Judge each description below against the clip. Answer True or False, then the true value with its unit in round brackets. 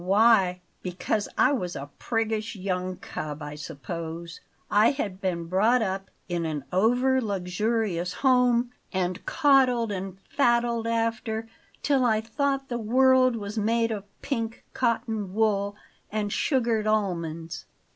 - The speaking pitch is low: False (215 Hz)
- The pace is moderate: False (130 wpm)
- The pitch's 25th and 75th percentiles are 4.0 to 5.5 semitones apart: True (4.4 semitones)